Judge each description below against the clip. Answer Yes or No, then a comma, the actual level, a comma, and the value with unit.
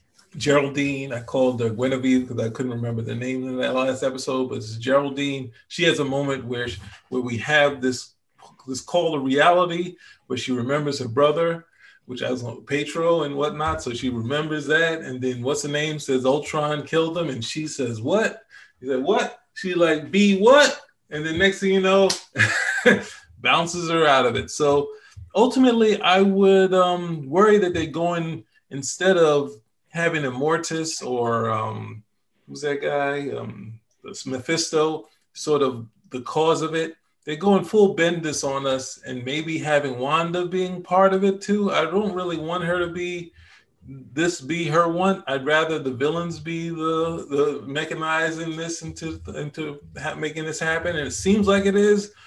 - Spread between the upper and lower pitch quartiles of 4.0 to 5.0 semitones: Yes, average, 4.5 semitones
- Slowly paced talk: No, average, 175 wpm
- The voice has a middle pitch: Yes, medium, 155 Hz